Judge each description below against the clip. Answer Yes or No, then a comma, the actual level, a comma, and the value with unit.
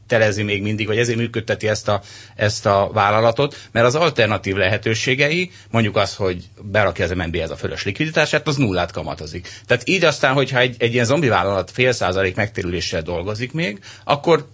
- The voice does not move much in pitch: No, average, 4.2 semitones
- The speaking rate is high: Yes, fast, 175 wpm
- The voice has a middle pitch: No, low, 110 Hz